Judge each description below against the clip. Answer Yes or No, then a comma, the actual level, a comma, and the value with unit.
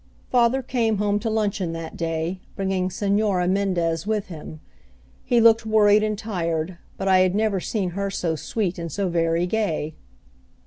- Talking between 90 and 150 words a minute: No, average, 165 wpm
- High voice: Yes, high, 195 Hz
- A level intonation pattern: No, average, 4.0 semitones